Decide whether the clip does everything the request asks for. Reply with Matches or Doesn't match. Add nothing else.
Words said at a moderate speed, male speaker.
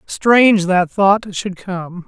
Matches